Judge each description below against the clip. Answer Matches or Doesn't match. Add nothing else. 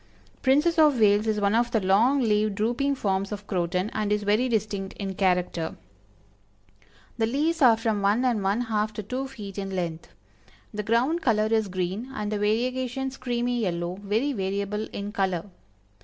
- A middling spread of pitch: Matches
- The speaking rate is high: Doesn't match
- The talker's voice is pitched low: Doesn't match